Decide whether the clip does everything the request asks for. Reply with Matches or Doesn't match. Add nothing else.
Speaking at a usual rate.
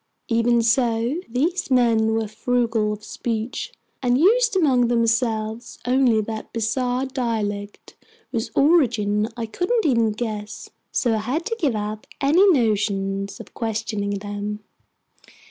Doesn't match